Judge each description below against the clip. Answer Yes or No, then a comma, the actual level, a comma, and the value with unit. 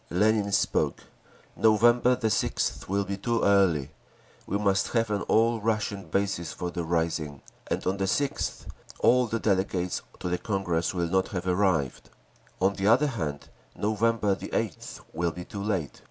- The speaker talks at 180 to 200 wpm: No, average, 155 wpm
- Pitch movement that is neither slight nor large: Yes, average, 3.6 semitones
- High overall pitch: No, low, 100 Hz